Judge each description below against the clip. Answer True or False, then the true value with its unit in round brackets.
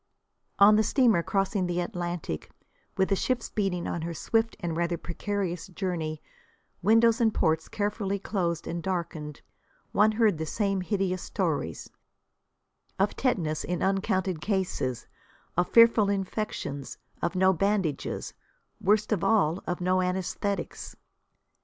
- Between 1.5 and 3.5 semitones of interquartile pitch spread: True (3.2 semitones)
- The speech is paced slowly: True (130 wpm)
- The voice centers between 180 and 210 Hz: True (190 Hz)